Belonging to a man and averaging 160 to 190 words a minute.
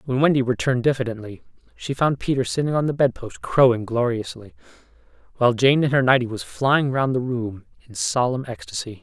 Yes: male; average, 180 wpm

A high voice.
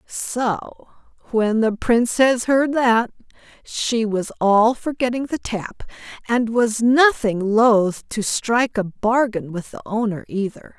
Yes: high, 230 Hz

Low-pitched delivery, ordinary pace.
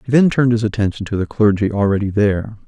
No: low, 105 Hz; fast, 225 wpm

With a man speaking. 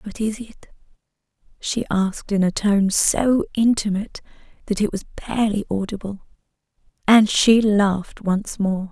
No: female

